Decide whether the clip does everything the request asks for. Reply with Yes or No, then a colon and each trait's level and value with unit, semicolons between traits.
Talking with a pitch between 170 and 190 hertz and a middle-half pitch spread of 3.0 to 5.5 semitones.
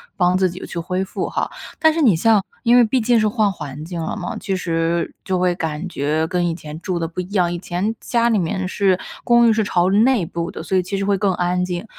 Yes: medium, 185 Hz; average, 3.5 semitones